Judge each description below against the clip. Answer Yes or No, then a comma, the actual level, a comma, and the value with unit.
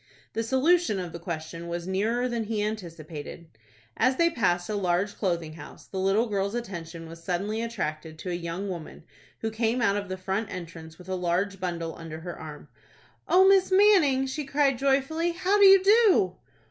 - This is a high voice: Yes, high, 200 Hz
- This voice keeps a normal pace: Yes, average, 185 wpm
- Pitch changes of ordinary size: No, wide, 7.3 semitones